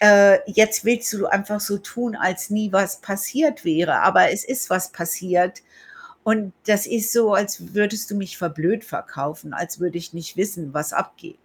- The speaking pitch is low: No, high, 200 Hz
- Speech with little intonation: No, average, 3.2 semitones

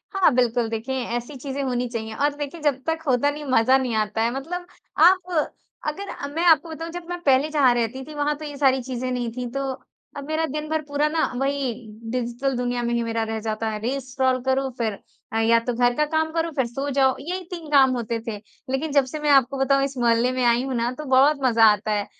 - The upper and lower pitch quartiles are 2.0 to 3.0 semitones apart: No, average, 3.7 semitones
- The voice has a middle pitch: No, very high, 265 Hz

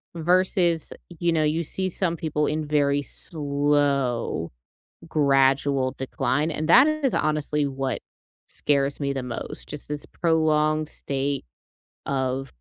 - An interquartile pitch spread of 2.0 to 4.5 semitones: Yes, narrow, 2.5 semitones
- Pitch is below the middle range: No, medium, 150 Hz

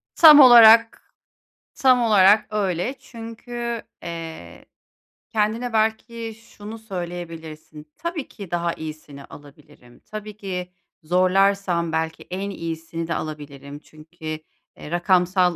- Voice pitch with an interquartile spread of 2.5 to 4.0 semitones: No, wide, 5.4 semitones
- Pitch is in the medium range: Yes, medium, 180 Hz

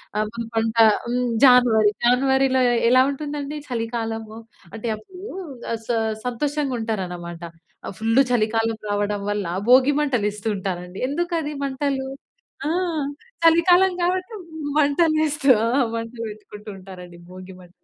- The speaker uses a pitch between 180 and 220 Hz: No, high, 235 Hz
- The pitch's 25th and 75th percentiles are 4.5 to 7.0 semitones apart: Yes, average, 5.2 semitones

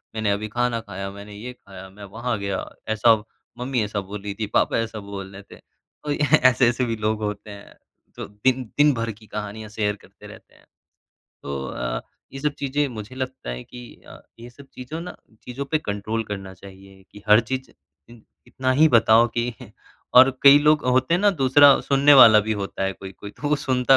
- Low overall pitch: Yes, low, 115 Hz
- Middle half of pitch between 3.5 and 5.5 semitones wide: Yes, average, 4.3 semitones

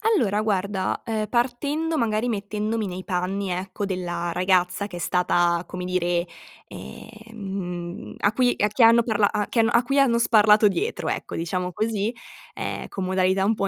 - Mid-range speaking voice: No, high, 200 Hz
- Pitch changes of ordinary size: Yes, average, 3.6 semitones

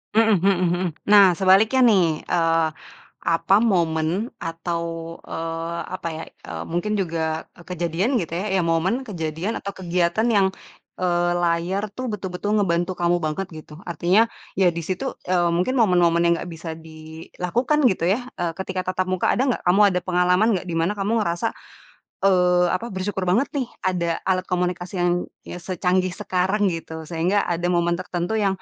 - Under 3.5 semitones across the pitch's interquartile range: Yes, narrow, 2.4 semitones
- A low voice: No, medium, 180 Hz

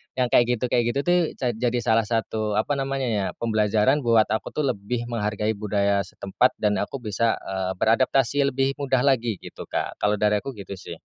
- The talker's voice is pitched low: Yes, low, 115 Hz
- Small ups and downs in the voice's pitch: No, average, 3.5 semitones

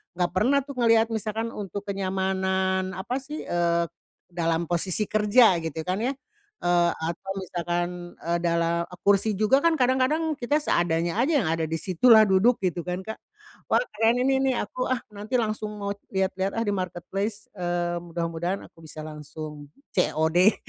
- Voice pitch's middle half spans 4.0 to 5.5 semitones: Yes, average, 4.3 semitones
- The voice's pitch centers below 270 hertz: Yes, high, 190 Hz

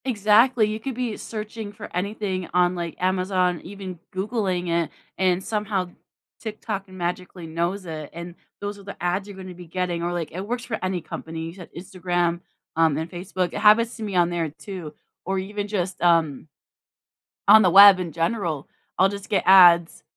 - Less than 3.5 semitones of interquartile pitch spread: Yes, average, 2.8 semitones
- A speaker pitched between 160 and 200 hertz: Yes, medium, 185 Hz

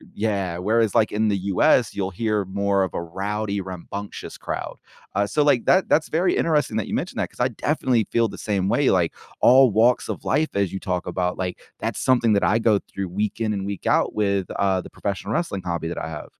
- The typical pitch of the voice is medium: No, low, 100 Hz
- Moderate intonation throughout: Yes, average, 3.1 semitones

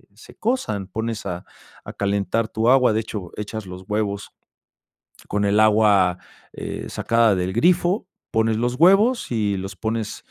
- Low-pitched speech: Yes, low, 110 Hz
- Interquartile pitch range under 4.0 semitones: Yes, narrow, 2.6 semitones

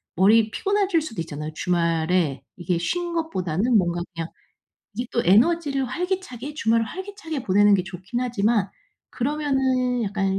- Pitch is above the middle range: Yes, high, 230 Hz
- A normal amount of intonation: No, wide, 8.1 semitones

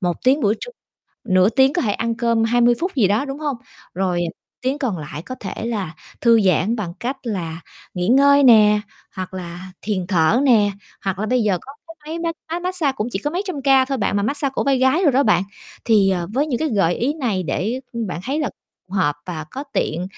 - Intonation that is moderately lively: No, wide, 6.4 semitones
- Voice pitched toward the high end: Yes, high, 230 Hz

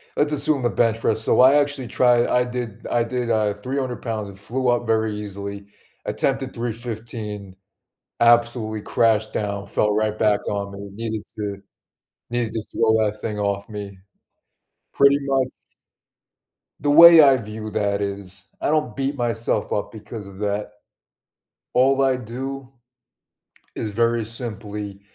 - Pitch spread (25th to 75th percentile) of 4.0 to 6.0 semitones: No, average, 3.2 semitones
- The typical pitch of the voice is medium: No, low, 115 Hz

